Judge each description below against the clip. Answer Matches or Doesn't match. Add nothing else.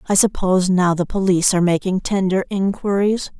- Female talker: Matches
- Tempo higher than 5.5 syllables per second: Matches